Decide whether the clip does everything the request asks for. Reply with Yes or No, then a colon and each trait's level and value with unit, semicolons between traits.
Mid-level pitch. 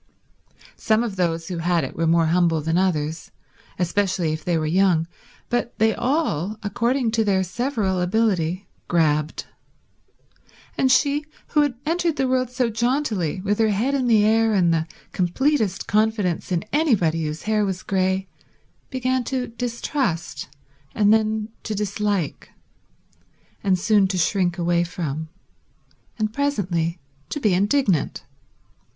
No: high, 200 Hz